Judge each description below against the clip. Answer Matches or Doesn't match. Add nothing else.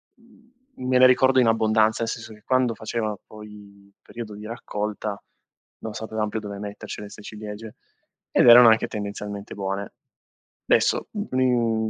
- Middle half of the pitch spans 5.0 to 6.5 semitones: Doesn't match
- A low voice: Matches